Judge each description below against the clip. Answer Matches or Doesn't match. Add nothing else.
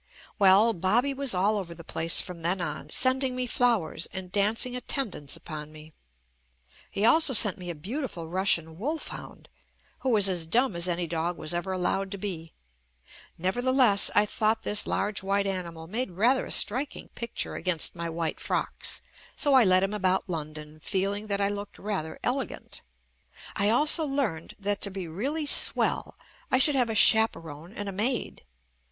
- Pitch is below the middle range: Doesn't match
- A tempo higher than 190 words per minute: Doesn't match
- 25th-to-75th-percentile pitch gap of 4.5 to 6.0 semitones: Matches